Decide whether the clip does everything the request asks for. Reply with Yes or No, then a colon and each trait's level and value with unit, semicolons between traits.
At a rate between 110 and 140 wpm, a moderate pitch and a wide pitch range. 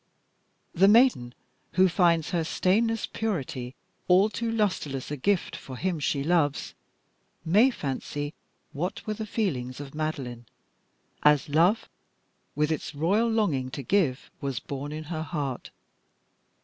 Yes: slow, 135 wpm; medium, 160 Hz; wide, 6.1 semitones